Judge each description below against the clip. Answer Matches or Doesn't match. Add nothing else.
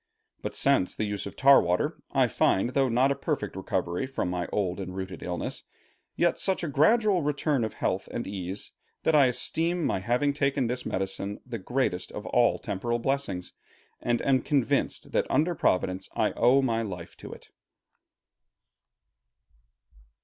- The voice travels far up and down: Matches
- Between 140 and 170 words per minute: Matches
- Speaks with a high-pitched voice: Doesn't match